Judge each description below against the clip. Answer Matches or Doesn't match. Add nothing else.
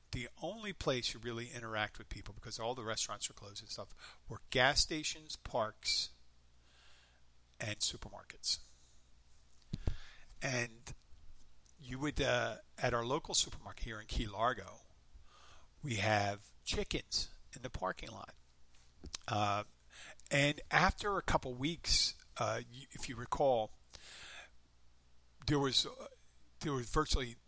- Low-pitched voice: Matches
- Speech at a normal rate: Doesn't match